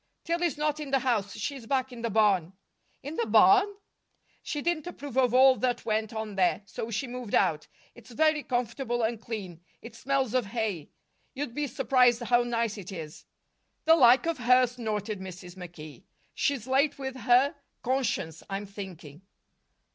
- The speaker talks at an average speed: Yes, average, 170 wpm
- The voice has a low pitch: No, high, 240 Hz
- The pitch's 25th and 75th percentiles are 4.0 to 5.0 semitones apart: Yes, average, 4.4 semitones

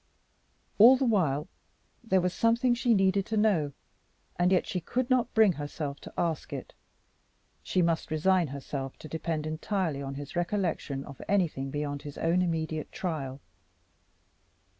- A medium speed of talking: Yes, average, 150 wpm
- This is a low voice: No, medium, 170 Hz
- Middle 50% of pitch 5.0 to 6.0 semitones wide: Yes, average, 5.3 semitones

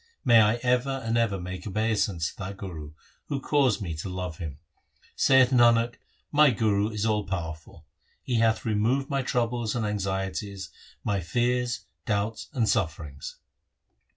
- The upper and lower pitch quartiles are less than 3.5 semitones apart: No, average, 4.2 semitones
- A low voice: Yes, low, 105 Hz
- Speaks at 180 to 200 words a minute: No, average, 150 wpm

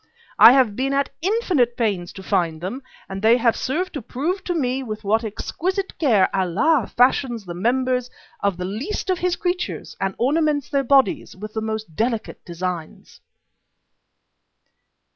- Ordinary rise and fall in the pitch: No, wide, 6.2 semitones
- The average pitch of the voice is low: No, high, 245 Hz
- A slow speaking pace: No, average, 160 wpm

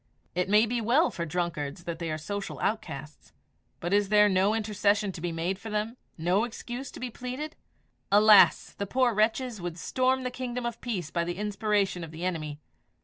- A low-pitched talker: No, high, 205 Hz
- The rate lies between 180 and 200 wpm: Yes, average, 195 wpm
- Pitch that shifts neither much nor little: Yes, average, 4.9 semitones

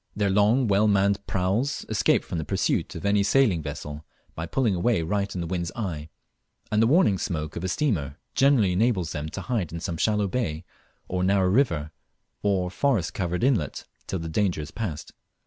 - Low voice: Yes, very low, 95 Hz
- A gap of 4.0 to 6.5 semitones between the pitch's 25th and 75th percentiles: Yes, average, 4.5 semitones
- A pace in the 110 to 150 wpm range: No, average, 190 wpm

